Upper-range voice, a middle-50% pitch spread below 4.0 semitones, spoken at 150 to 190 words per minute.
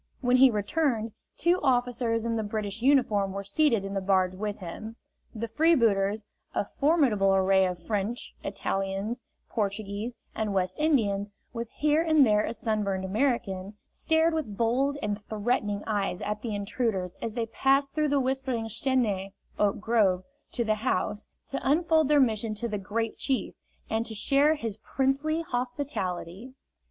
No: high, 225 Hz; average, 4.7 semitones; average, 155 wpm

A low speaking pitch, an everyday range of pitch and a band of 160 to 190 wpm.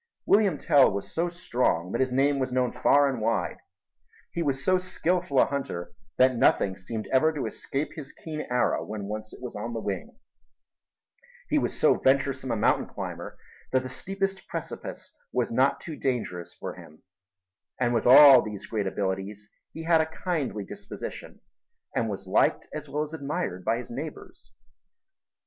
No: low, 130 Hz; wide, 6.3 semitones; average, 170 wpm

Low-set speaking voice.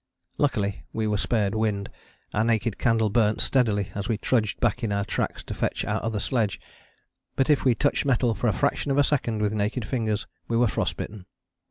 Yes: low, 110 Hz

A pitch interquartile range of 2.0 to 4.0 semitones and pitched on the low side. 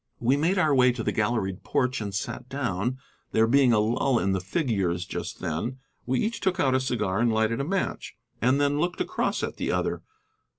No: average, 4.5 semitones; low, 125 Hz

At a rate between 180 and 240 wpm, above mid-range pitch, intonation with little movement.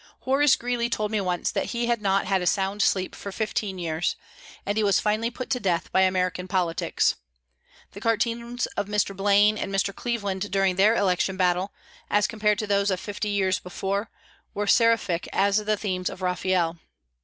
Yes: average, 185 wpm; high, 200 Hz; narrow, 2.3 semitones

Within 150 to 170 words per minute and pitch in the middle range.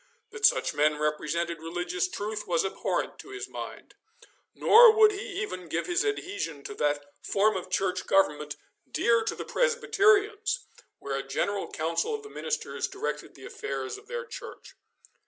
No: average, 160 wpm; high, 210 Hz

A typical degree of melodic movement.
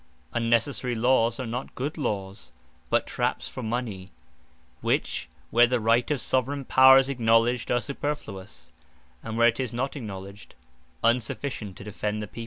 Yes: average, 3.0 semitones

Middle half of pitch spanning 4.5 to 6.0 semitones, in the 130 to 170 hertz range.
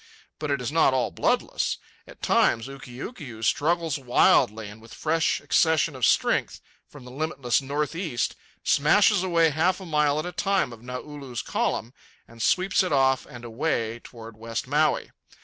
Yes: average, 4.9 semitones; medium, 140 Hz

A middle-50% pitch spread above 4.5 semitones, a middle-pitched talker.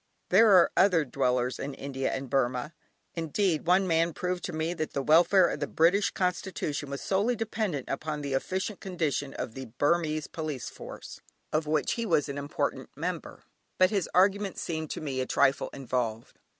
Yes: average, 4.9 semitones; medium, 155 Hz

